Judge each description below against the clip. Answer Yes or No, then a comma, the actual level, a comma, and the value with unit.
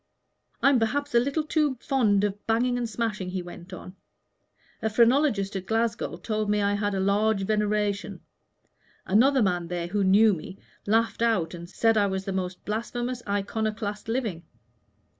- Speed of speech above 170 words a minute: No, average, 160 wpm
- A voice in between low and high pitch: No, high, 210 Hz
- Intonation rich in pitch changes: No, average, 3.1 semitones